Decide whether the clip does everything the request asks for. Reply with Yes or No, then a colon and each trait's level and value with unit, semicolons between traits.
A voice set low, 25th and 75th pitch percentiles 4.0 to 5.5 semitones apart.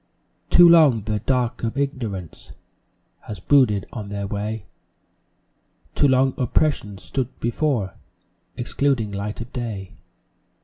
Yes: low, 115 Hz; average, 4.6 semitones